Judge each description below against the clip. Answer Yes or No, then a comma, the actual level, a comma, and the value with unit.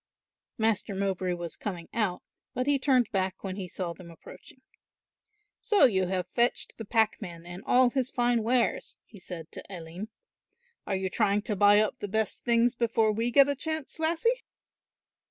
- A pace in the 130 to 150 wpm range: No, average, 170 wpm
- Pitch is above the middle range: Yes, high, 215 Hz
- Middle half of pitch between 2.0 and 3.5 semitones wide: No, average, 4.5 semitones